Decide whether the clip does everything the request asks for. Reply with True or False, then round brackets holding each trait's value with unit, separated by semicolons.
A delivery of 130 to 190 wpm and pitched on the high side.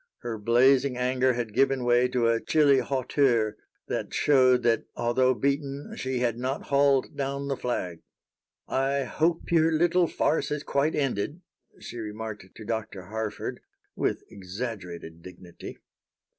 False (140 wpm; 125 Hz)